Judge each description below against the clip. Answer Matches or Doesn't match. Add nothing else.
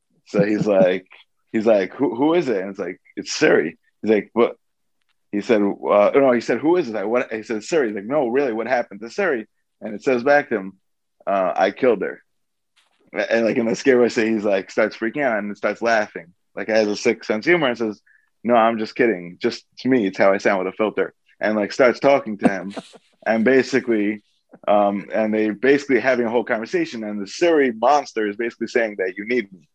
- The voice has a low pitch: Matches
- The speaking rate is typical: Doesn't match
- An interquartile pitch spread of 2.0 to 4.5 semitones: Matches